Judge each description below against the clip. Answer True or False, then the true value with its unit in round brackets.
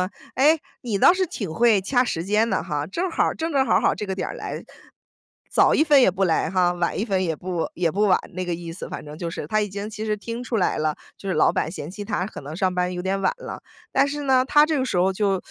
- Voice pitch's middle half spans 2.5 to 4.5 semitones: False (5.3 semitones)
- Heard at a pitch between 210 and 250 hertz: False (195 Hz)